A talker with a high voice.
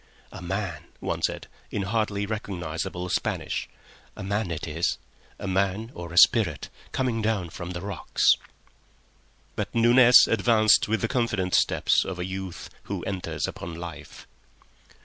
No: very low, 95 Hz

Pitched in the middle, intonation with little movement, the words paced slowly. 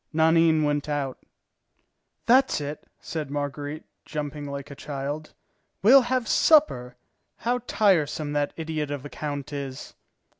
Yes: medium, 150 Hz; narrow, 2.2 semitones; slow, 125 wpm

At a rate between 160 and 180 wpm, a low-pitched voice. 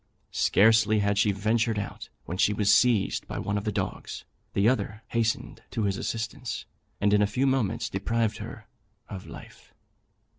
Yes: average, 170 wpm; low, 105 Hz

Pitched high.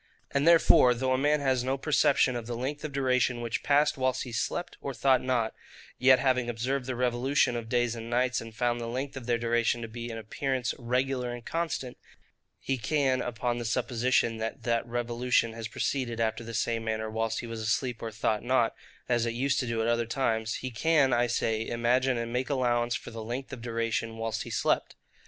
No: low, 120 Hz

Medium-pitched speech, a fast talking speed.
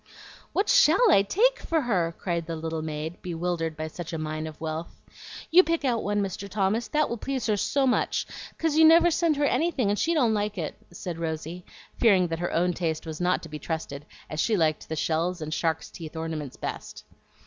Yes: medium, 180 Hz; fast, 215 wpm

